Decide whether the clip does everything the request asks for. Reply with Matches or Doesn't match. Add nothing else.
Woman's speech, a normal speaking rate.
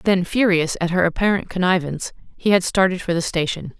Matches